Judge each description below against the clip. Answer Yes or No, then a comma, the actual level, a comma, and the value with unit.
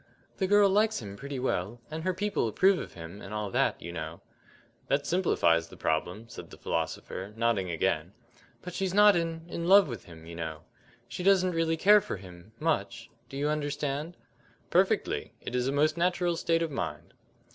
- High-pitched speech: No, medium, 145 Hz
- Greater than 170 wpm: Yes, average, 190 wpm